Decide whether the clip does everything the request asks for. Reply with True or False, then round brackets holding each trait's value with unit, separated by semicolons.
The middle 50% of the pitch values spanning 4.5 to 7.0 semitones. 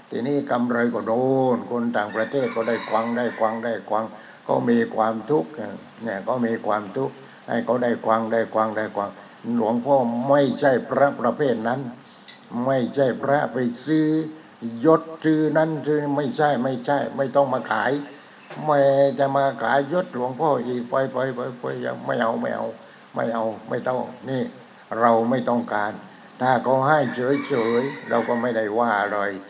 False (3.6 semitones)